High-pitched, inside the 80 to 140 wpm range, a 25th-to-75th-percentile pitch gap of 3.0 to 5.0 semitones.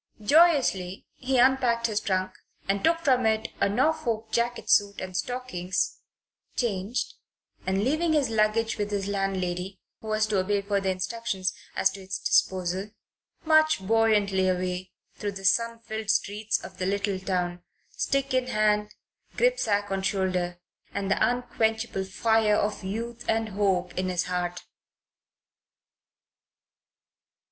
Yes: high, 205 Hz; slow, 135 wpm; average, 3.5 semitones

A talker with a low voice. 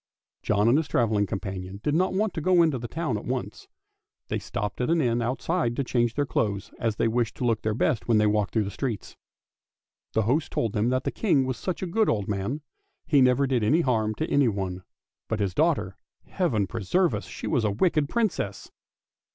Yes: low, 120 Hz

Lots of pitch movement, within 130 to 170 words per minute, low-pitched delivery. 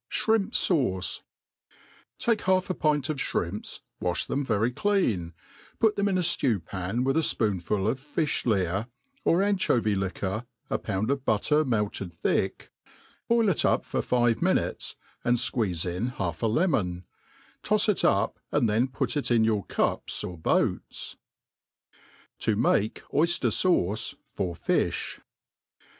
Yes: wide, 7.8 semitones; average, 150 wpm; low, 115 Hz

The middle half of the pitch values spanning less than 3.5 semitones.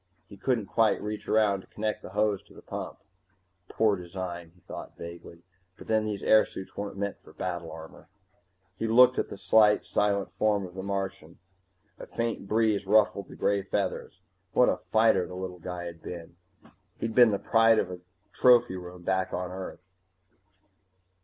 Yes: average, 3.1 semitones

